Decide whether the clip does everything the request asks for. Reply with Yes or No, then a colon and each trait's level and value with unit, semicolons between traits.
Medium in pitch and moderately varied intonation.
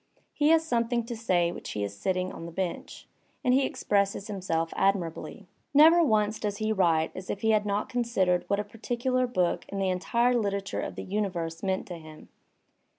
No: high, 200 Hz; average, 4.4 semitones